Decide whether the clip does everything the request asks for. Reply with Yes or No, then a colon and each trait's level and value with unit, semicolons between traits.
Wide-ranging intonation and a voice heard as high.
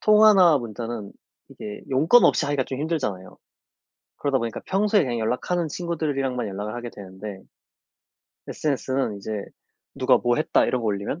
No: wide, 6.6 semitones; low, 130 Hz